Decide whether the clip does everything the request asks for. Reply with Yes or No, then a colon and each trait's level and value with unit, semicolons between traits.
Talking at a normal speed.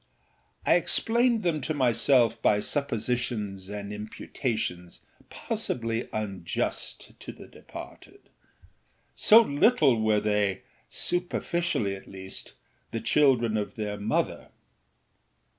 No: slow, 90 wpm